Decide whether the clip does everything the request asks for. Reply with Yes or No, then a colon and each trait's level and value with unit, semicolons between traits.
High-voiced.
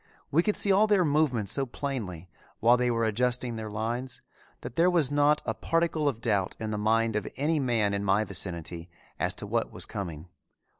No: low, 120 Hz